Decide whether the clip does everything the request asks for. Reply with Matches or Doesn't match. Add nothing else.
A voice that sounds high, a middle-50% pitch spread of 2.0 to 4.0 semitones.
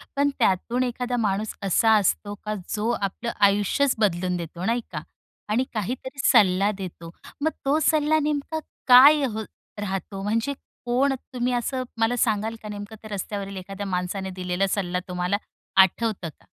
Doesn't match